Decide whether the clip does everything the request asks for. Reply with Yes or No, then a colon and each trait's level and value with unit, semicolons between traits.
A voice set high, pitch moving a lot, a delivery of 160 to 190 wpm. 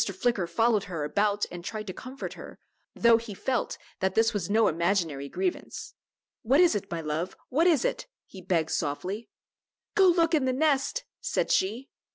Yes: high, 215 Hz; wide, 6.4 semitones; average, 180 wpm